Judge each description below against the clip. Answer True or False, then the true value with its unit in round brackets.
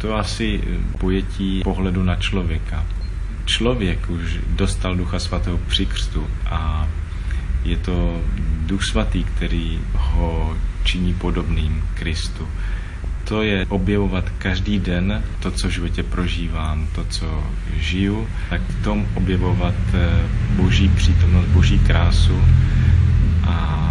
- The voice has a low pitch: True (90 Hz)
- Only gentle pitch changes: True (2.3 semitones)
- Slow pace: True (110 wpm)